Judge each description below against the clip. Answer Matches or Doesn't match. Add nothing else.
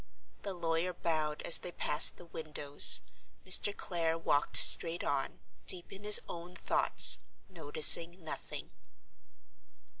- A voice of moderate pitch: Matches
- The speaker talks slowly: Matches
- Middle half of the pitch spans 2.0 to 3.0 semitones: Matches